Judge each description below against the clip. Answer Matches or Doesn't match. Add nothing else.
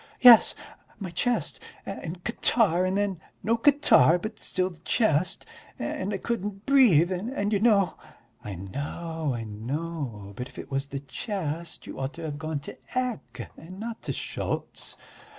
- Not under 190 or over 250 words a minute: Doesn't match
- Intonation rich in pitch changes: Matches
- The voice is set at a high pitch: Doesn't match